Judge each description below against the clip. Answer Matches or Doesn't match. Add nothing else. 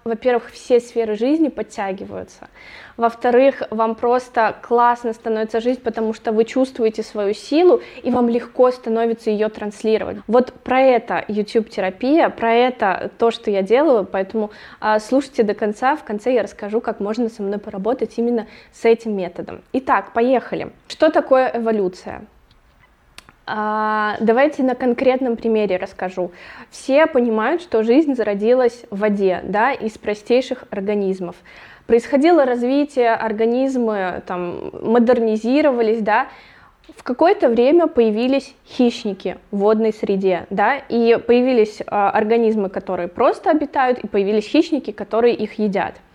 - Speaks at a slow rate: Doesn't match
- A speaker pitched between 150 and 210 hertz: Doesn't match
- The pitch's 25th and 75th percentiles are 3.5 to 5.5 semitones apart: Doesn't match